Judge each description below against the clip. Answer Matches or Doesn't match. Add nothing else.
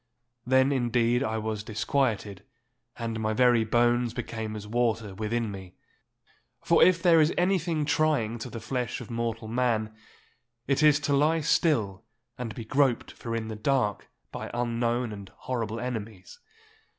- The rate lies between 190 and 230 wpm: Doesn't match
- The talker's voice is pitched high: Doesn't match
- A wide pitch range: Doesn't match